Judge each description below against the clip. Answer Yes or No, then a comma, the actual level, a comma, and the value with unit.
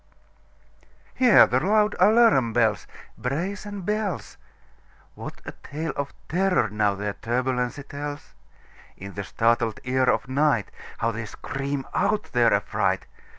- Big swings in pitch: Yes, wide, 7.8 semitones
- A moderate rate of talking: No, slow, 110 wpm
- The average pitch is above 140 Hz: No, low, 135 Hz